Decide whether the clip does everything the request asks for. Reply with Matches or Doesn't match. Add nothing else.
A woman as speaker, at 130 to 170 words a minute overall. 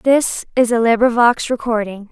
Matches